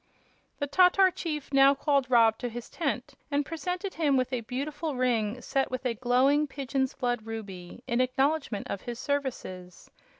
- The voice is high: Yes, very high, 260 Hz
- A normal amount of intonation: Yes, average, 3.2 semitones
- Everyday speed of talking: Yes, average, 165 wpm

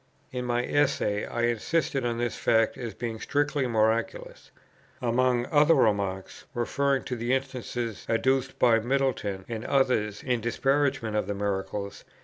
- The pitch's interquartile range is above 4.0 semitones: No, average, 3.2 semitones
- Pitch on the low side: Yes, low, 120 Hz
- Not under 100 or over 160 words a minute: Yes, average, 145 wpm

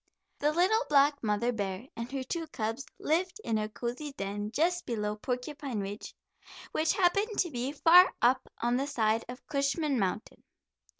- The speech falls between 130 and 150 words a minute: No, average, 165 wpm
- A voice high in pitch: Yes, very high, 260 Hz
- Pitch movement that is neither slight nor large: No, wide, 5.7 semitones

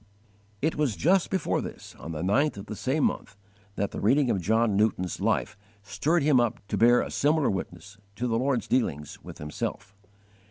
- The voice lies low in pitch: Yes, low, 115 Hz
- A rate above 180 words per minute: Yes, average, 190 wpm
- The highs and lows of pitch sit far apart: Yes, wide, 6.1 semitones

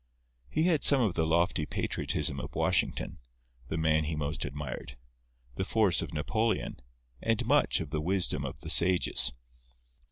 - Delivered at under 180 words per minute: Yes, average, 155 wpm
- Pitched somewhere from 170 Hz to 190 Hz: No, very low, 85 Hz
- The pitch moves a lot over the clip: Yes, wide, 6.3 semitones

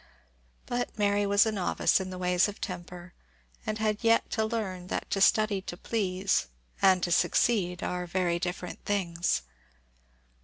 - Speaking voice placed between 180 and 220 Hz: Yes, high, 190 Hz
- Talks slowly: No, average, 155 wpm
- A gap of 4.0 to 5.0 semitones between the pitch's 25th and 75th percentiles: No, average, 3.0 semitones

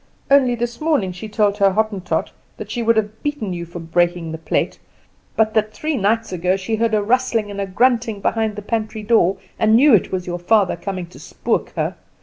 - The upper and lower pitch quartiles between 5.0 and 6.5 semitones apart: No, average, 3.5 semitones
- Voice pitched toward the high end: Yes, high, 215 Hz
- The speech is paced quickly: Yes, fast, 210 wpm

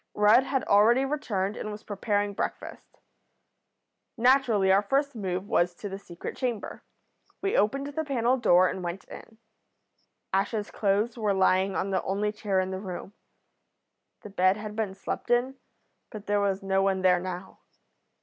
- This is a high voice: Yes, high, 205 Hz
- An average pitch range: Yes, average, 3.4 semitones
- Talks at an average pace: Yes, average, 160 wpm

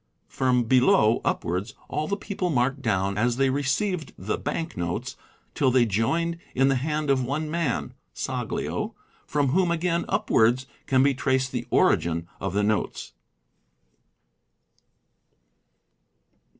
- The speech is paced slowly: Yes, slow, 130 wpm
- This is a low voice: Yes, low, 130 Hz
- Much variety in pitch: No, average, 4.7 semitones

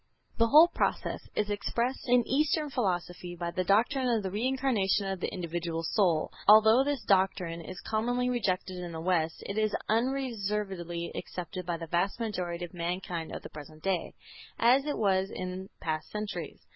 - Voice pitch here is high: Yes, high, 195 Hz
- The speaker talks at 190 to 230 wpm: No, average, 170 wpm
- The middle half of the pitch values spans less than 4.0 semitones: No, average, 4.9 semitones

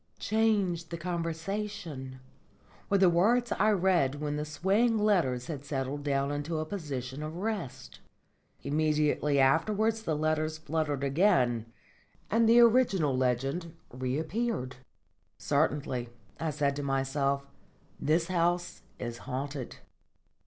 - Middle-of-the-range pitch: Yes, medium, 155 Hz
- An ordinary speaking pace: No, slow, 115 wpm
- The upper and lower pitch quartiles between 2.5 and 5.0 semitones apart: No, wide, 5.4 semitones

